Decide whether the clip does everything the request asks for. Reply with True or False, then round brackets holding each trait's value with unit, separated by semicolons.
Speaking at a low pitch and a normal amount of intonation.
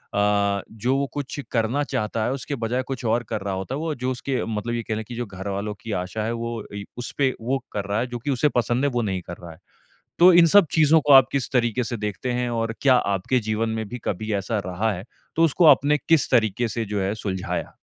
True (115 Hz; 4.1 semitones)